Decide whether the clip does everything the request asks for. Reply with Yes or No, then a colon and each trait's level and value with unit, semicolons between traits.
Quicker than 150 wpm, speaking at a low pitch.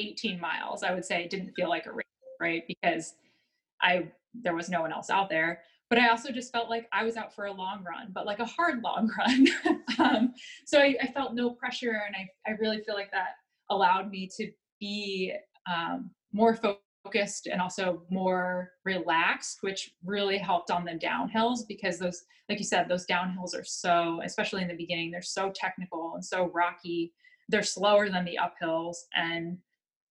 No: average, 190 wpm; high, 195 Hz